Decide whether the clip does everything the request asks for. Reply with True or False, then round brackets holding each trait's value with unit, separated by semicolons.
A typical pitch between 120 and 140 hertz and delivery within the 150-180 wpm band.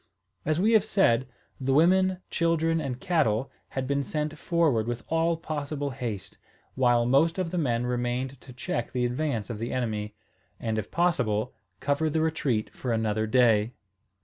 True (135 Hz; 165 wpm)